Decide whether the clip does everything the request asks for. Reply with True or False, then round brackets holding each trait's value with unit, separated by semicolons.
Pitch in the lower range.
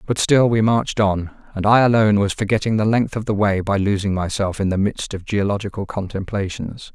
True (105 Hz)